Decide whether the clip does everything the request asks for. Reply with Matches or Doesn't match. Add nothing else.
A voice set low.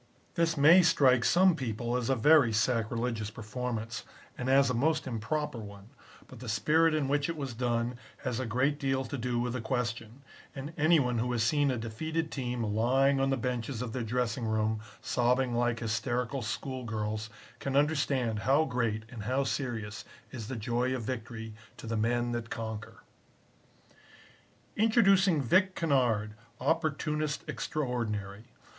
Matches